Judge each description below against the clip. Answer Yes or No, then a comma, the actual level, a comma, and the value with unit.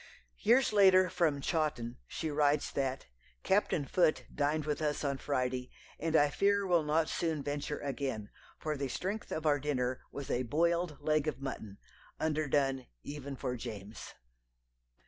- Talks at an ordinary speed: Yes, average, 150 wpm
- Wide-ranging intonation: No, average, 3.0 semitones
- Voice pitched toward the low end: No, medium, 145 Hz